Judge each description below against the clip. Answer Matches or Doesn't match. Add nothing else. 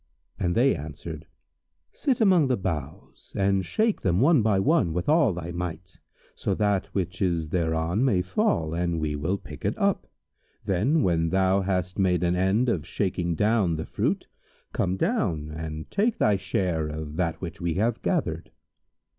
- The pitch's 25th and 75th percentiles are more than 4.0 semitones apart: Doesn't match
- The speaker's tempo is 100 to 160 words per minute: Doesn't match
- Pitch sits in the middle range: Doesn't match